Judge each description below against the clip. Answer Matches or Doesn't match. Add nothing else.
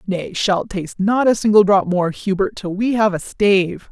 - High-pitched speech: Matches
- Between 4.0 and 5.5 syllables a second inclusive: Matches